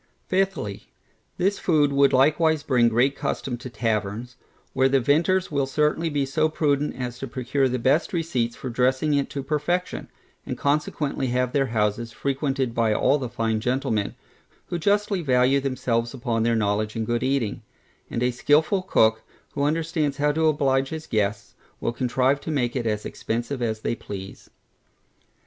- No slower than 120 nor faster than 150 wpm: No, average, 165 wpm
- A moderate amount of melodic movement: Yes, average, 3.9 semitones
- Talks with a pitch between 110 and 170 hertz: Yes, low, 135 Hz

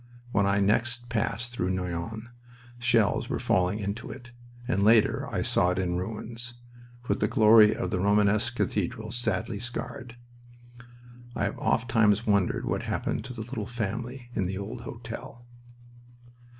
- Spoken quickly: No, average, 150 wpm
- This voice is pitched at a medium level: No, low, 110 Hz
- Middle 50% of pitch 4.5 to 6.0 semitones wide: No, average, 3.1 semitones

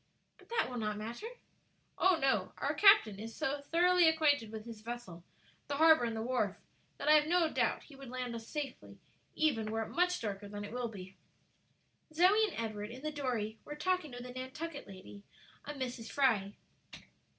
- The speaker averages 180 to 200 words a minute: Yes, average, 190 wpm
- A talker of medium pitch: No, very high, 255 Hz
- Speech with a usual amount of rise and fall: No, wide, 5.7 semitones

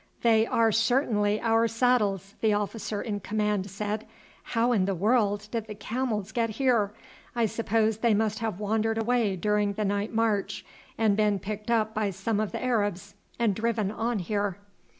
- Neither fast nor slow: Yes, average, 170 wpm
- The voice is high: Yes, high, 215 Hz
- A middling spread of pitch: No, narrow, 1.8 semitones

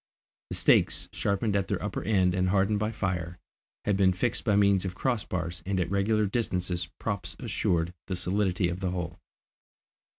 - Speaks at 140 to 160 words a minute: No, average, 175 wpm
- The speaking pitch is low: Yes, very low, 95 Hz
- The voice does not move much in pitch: Yes, narrow, 2.3 semitones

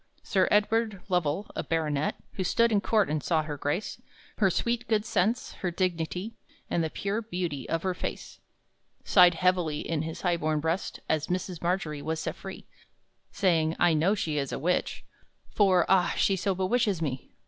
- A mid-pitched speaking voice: Yes, medium, 180 Hz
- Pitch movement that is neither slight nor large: Yes, average, 3.8 semitones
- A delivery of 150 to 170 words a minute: No, average, 180 wpm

